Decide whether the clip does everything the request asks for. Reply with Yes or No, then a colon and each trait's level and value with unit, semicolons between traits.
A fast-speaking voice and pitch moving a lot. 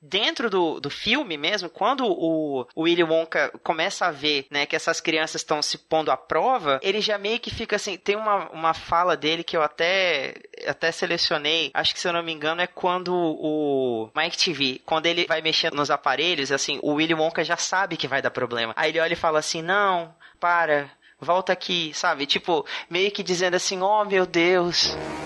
No: fast, 200 wpm; average, 3.0 semitones